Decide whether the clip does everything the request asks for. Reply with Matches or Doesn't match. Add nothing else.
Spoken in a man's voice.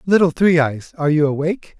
Matches